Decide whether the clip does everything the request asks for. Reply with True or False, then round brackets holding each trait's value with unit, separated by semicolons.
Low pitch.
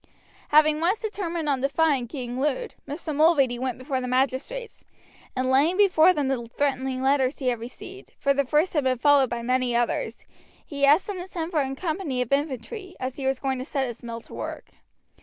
False (275 Hz)